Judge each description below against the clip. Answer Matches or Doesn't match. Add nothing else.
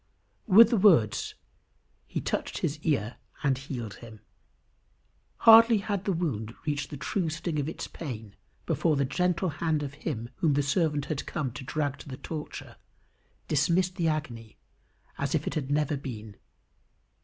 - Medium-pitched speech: Matches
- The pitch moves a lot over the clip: Doesn't match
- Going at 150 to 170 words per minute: Matches